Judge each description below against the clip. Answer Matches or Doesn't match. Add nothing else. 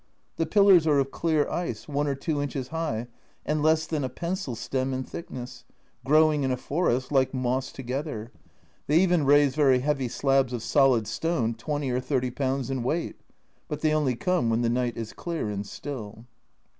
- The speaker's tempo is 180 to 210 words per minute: Matches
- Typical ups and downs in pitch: Matches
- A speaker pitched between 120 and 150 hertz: Matches